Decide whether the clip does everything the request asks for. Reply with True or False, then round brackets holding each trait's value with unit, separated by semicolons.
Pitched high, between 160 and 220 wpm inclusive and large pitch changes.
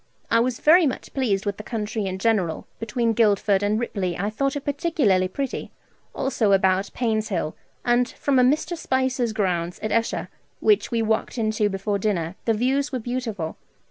False (220 Hz; 175 wpm; 4.4 semitones)